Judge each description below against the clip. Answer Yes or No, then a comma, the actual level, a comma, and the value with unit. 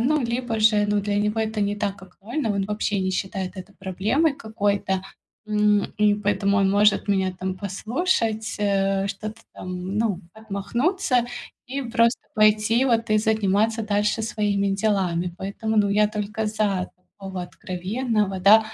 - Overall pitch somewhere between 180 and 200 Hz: No, high, 210 Hz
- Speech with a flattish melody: Yes, narrow, 2.1 semitones